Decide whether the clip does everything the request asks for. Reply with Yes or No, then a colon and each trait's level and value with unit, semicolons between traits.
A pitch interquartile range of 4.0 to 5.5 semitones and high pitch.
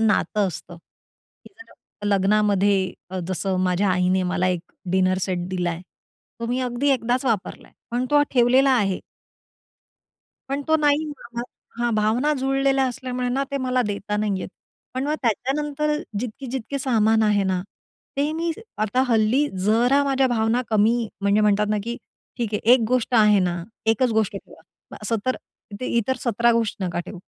Yes: average, 4.3 semitones; high, 230 Hz